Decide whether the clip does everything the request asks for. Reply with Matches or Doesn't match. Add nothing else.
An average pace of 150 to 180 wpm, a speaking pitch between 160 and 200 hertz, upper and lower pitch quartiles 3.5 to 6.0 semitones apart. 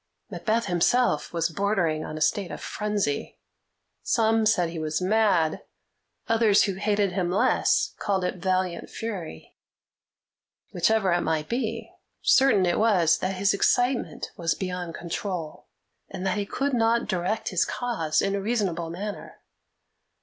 Doesn't match